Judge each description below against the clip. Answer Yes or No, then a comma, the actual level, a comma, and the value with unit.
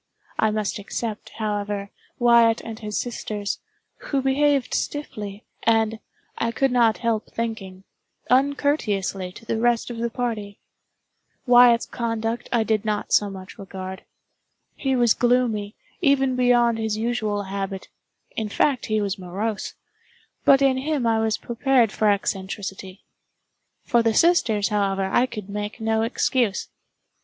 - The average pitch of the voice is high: Yes, high, 225 Hz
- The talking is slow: Yes, slow, 130 wpm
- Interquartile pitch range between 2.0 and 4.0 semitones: Yes, average, 2.9 semitones